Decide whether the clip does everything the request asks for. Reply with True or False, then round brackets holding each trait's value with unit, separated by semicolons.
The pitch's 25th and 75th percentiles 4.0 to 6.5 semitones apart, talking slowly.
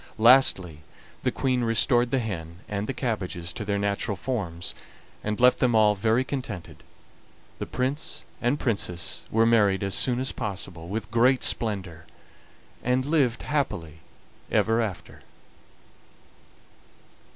True (4.6 semitones; 130 wpm)